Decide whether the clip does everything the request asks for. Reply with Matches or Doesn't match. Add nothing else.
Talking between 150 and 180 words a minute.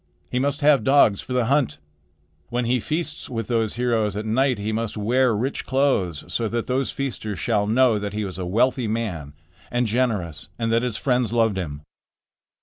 Doesn't match